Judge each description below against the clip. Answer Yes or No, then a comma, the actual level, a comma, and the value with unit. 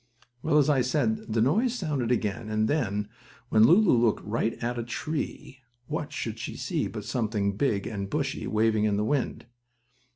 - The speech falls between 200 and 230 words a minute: No, average, 175 wpm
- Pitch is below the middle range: Yes, low, 115 Hz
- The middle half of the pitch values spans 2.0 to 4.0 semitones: No, average, 4.7 semitones